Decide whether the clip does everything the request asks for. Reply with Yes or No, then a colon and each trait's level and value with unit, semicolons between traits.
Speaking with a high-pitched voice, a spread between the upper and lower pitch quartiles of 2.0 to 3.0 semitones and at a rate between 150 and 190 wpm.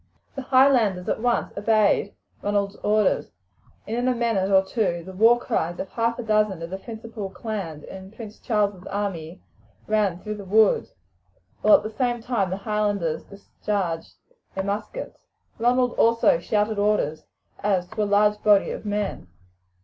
Yes: high, 210 Hz; average, 2.7 semitones; average, 160 wpm